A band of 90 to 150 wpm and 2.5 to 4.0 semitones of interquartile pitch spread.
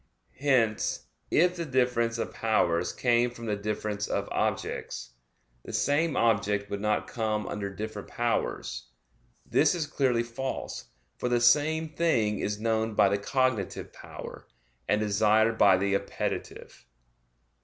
Yes: slow, 135 wpm; average, 3.3 semitones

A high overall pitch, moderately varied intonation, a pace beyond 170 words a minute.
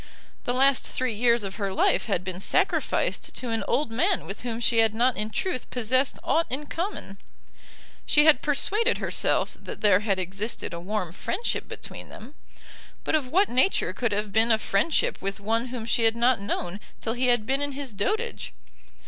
Yes: high, 235 Hz; average, 4.7 semitones; average, 190 wpm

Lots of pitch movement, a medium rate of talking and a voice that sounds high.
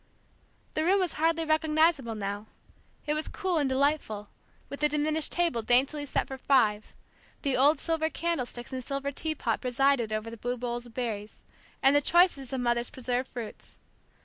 No: average, 4.4 semitones; average, 165 wpm; very high, 270 Hz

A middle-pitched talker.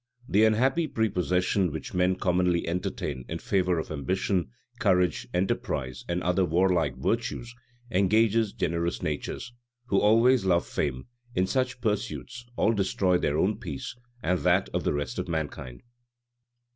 No: very low, 90 Hz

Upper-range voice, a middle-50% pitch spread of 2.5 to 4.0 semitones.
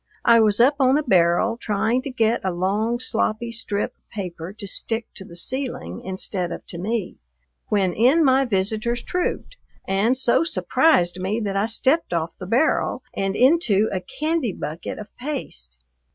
No: high, 220 Hz; average, 5.0 semitones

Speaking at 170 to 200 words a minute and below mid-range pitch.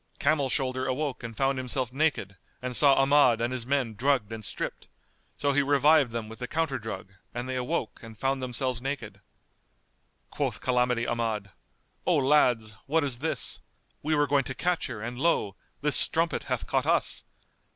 Yes: average, 175 wpm; low, 130 Hz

